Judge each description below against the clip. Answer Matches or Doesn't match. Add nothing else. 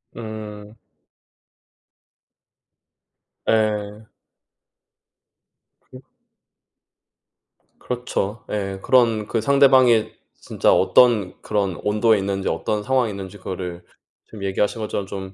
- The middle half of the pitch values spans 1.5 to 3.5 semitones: Matches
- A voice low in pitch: Matches